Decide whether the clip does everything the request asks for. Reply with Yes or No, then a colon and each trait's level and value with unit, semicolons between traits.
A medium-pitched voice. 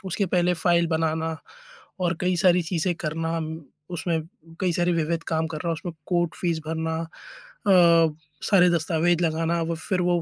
Yes: medium, 170 Hz